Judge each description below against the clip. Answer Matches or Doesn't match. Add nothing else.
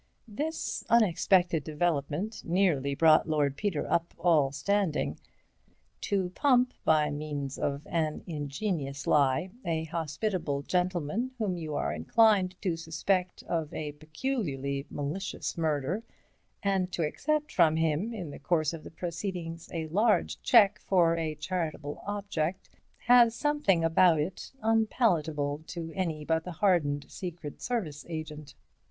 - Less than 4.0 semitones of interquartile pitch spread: Doesn't match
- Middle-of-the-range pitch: Matches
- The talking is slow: Matches